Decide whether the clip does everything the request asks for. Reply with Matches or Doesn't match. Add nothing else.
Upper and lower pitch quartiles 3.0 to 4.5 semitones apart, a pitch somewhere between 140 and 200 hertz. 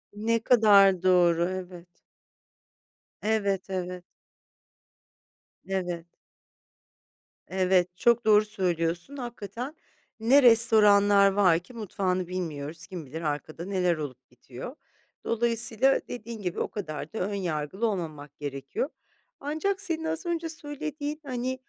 Doesn't match